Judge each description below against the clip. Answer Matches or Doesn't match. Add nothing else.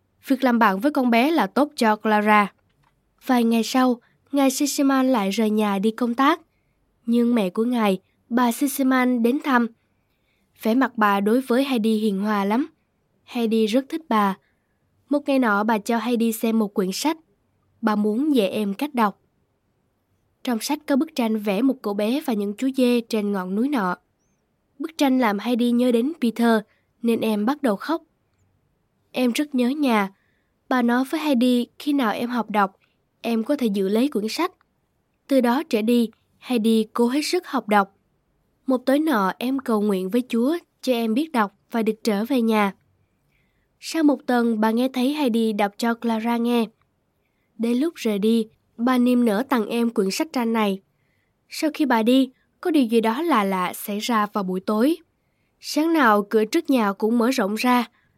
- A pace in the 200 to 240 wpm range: Doesn't match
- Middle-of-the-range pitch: Doesn't match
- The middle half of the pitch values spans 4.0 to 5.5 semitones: Doesn't match